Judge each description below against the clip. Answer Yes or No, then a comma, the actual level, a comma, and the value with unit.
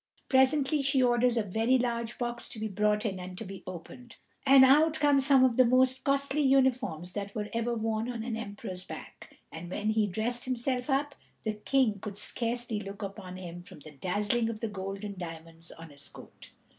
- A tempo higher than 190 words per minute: Yes, average, 200 wpm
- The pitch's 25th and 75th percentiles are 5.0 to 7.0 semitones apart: No, average, 4.6 semitones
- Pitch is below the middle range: No, high, 225 Hz